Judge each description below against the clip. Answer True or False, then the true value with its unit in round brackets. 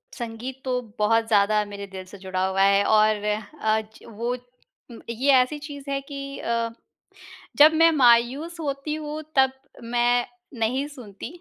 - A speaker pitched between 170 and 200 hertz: False (240 Hz)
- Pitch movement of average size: True (4.5 semitones)